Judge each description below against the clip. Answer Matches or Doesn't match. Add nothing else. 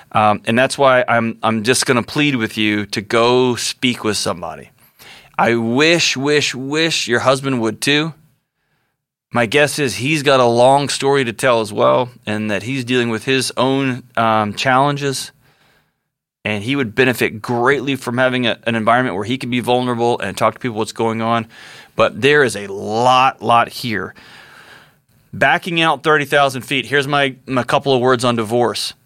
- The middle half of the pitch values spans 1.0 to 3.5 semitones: Matches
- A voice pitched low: Matches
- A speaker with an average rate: Matches